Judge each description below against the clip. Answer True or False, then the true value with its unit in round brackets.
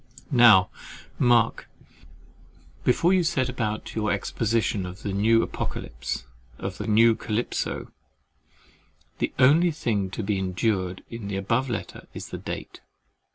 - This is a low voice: True (110 Hz)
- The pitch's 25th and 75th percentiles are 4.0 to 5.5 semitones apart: False (3.4 semitones)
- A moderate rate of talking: False (130 wpm)